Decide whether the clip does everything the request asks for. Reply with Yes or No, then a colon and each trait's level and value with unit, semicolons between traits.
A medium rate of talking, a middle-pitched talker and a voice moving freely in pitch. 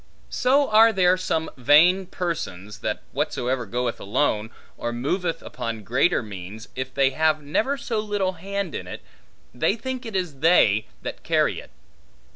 Yes: average, 155 wpm; medium, 160 Hz; wide, 8.0 semitones